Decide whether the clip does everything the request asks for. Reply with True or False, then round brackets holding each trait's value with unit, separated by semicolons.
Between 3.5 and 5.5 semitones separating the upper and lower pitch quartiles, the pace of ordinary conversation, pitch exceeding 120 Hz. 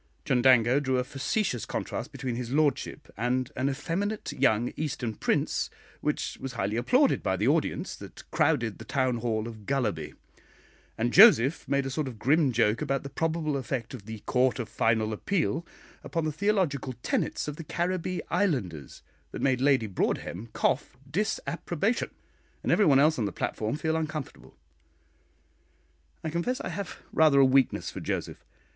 True (4.9 semitones; 160 wpm; 135 Hz)